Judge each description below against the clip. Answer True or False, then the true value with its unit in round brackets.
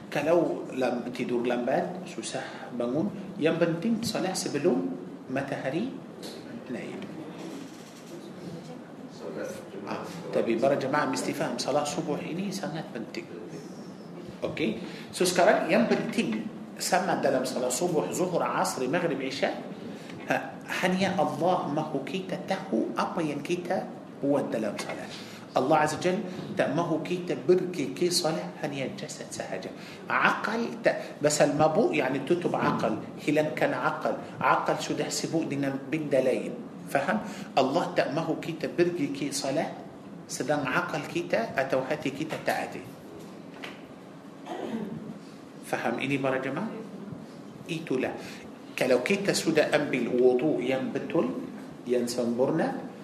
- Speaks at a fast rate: False (110 wpm)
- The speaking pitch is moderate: True (155 Hz)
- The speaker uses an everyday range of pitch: True (3.3 semitones)